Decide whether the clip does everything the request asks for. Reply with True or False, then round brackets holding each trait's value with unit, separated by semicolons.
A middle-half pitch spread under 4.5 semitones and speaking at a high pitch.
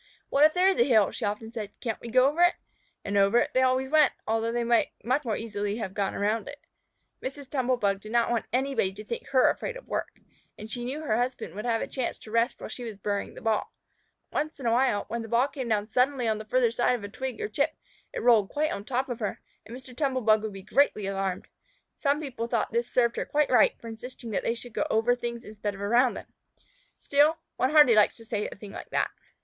True (3.3 semitones; 235 Hz)